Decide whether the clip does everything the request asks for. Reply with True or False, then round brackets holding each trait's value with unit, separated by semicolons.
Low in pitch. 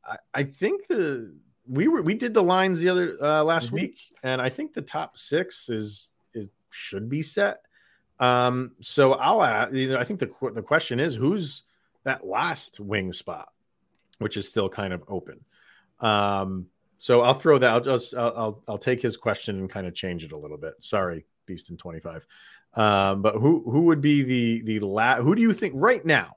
True (125 Hz)